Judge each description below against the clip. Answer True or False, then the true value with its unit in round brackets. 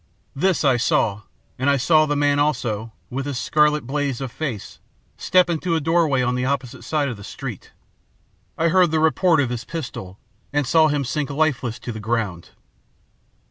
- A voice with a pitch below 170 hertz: True (140 Hz)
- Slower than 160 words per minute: False (180 wpm)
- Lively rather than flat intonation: False (4.2 semitones)